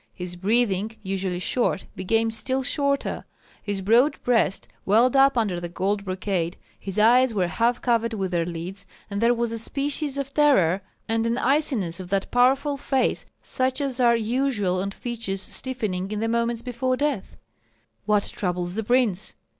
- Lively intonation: No, average, 4.8 semitones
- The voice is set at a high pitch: Yes, high, 225 Hz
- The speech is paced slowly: No, average, 165 wpm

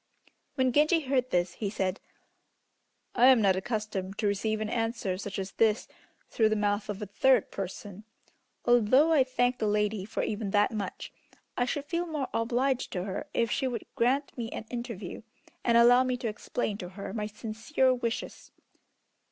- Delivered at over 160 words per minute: Yes, average, 175 wpm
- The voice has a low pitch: No, high, 225 Hz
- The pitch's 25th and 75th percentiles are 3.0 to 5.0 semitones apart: Yes, average, 3.6 semitones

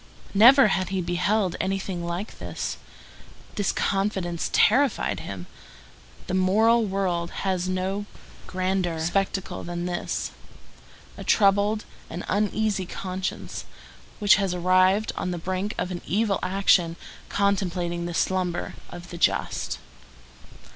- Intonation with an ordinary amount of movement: No, narrow, 2.3 semitones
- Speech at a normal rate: No, slow, 120 wpm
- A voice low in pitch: No, medium, 185 Hz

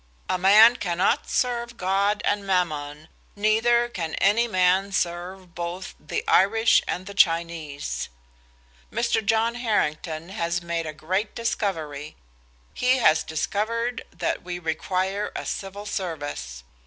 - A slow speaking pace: Yes, slow, 120 wpm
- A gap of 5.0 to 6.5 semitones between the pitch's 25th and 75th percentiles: No, average, 4.4 semitones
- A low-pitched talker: No, high, 190 Hz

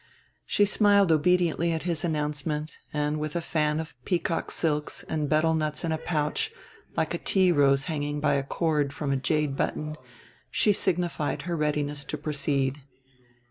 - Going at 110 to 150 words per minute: No, average, 165 wpm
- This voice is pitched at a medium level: Yes, medium, 155 Hz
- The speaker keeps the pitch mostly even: Yes, narrow, 2.3 semitones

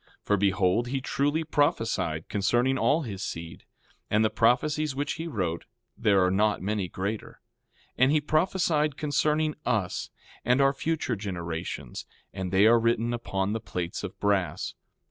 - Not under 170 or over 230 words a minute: No, average, 155 wpm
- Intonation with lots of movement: Yes, wide, 6.9 semitones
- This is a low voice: Yes, low, 115 Hz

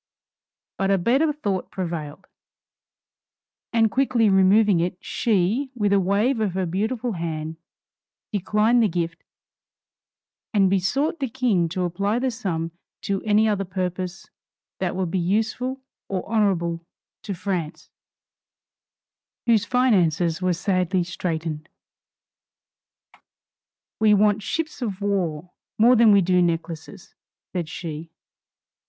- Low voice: No, high, 195 Hz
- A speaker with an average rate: No, slow, 120 wpm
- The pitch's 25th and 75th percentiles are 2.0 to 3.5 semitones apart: No, average, 4.1 semitones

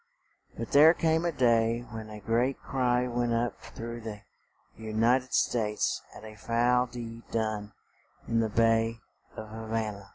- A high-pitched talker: No, low, 115 Hz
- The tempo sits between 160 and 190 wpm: Yes, average, 170 wpm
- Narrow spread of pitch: Yes, narrow, 1.8 semitones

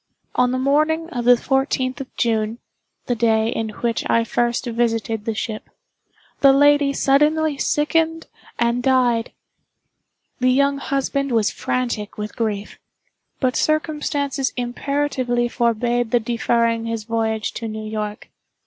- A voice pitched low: No, high, 245 Hz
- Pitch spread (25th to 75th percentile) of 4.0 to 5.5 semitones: No, average, 3.4 semitones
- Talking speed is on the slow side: Yes, slow, 130 wpm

